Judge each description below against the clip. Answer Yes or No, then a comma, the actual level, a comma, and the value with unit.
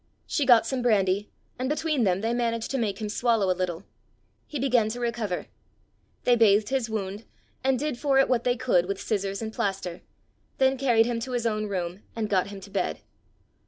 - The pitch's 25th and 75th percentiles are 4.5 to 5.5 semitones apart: No, average, 3.8 semitones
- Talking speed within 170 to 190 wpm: No, average, 200 wpm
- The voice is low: No, high, 225 Hz